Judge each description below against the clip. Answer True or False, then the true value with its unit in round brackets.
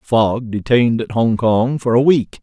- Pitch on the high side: False (115 Hz)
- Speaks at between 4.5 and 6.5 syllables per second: False (4.3 syllables/s)